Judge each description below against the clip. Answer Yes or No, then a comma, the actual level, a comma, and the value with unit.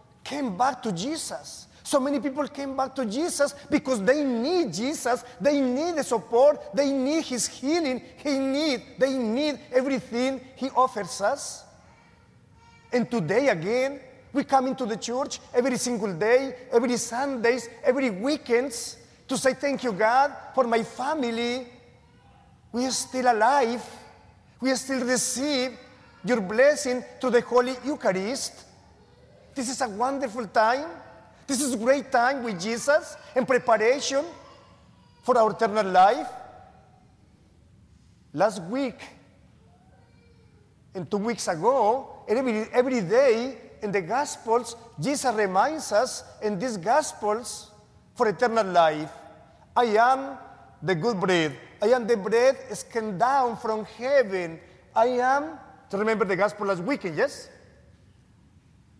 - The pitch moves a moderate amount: Yes, average, 3.3 semitones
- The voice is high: Yes, very high, 250 Hz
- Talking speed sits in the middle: No, slow, 130 wpm